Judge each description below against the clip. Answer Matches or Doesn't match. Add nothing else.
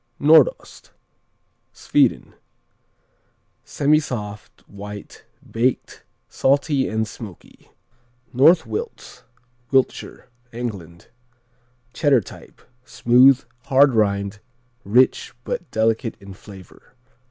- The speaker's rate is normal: Doesn't match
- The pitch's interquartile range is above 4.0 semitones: Matches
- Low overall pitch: Matches